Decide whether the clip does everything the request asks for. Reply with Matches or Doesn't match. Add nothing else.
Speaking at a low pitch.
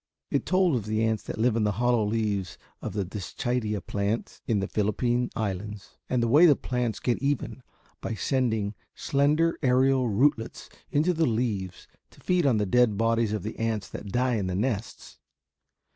Matches